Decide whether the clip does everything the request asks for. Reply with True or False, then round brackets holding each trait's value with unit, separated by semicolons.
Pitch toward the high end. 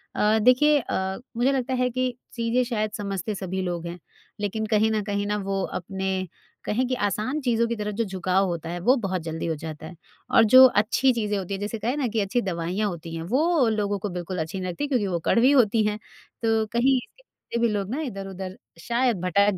True (210 Hz)